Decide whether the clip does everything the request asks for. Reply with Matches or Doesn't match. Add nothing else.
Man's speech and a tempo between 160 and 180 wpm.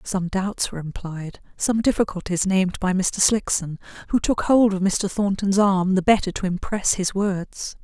Doesn't match